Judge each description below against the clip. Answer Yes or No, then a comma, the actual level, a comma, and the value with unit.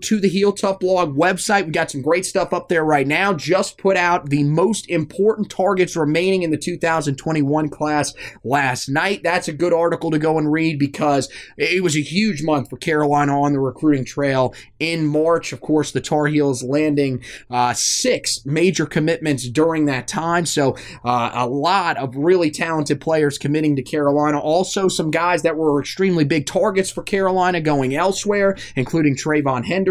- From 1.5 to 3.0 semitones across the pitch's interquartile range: No, average, 3.5 semitones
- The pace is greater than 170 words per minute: Yes, average, 180 wpm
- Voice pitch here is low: No, medium, 155 Hz